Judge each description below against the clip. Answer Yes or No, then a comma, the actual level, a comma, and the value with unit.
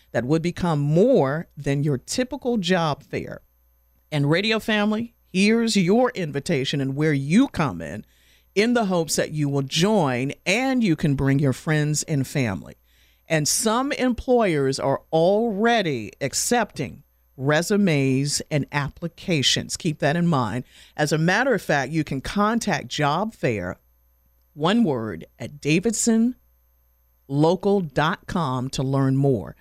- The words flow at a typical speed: No, slow, 130 wpm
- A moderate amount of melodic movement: No, wide, 6.9 semitones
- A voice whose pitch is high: No, medium, 150 Hz